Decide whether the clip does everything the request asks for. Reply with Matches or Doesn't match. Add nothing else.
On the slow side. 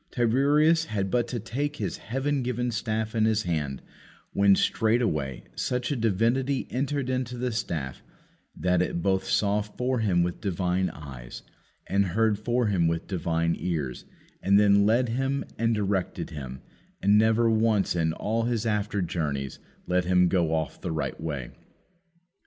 Doesn't match